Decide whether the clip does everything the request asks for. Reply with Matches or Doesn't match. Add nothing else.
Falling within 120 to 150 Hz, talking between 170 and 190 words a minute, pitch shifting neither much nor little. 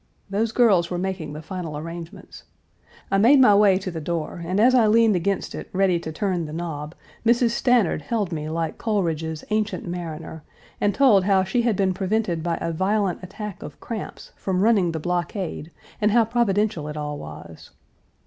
Doesn't match